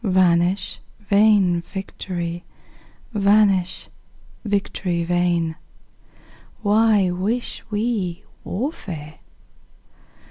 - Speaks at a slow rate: Yes, slow, 60 wpm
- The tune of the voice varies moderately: Yes, average, 3.1 semitones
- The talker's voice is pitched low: No, high, 190 Hz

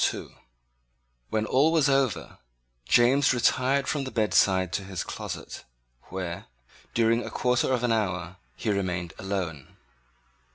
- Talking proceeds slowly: Yes, slow, 125 wpm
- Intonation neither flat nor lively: No, wide, 5.7 semitones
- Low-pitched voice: Yes, low, 110 Hz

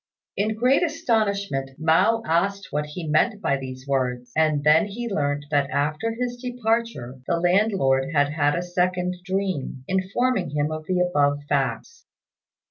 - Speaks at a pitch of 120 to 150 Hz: No, medium, 175 Hz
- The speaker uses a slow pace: No, average, 150 wpm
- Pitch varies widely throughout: Yes, wide, 6.4 semitones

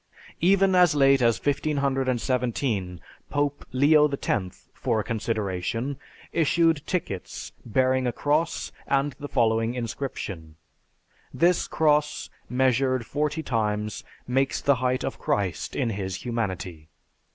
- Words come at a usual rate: No, slow, 115 wpm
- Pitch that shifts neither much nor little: Yes, average, 4.6 semitones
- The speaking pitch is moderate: No, low, 130 Hz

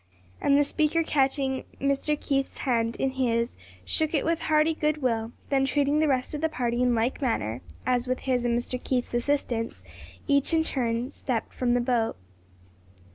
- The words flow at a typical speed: Yes, average, 180 wpm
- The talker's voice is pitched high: Yes, very high, 260 Hz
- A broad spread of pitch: No, average, 3.3 semitones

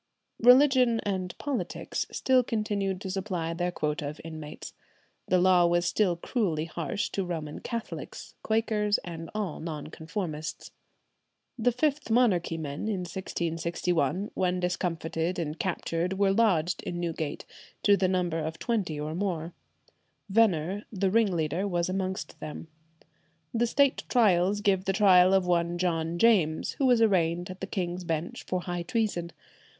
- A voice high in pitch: No, medium, 180 Hz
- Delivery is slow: No, average, 145 wpm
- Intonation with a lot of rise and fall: No, average, 3.7 semitones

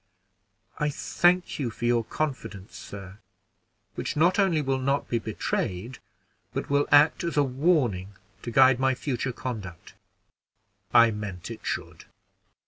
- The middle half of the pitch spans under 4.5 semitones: No, average, 5.2 semitones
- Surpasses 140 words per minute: No, slow, 135 wpm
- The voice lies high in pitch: No, low, 130 Hz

